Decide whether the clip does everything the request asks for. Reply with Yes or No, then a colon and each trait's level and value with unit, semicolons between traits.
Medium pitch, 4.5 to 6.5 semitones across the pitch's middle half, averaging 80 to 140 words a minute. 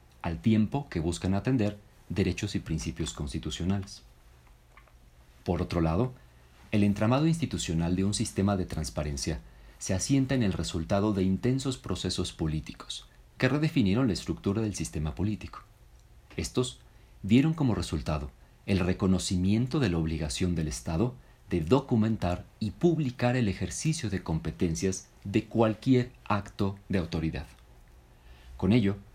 No: very low, 95 Hz; wide, 5.4 semitones; average, 130 wpm